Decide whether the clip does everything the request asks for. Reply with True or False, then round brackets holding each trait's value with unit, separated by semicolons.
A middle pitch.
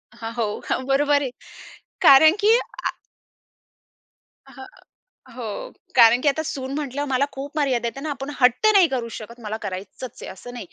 False (265 Hz)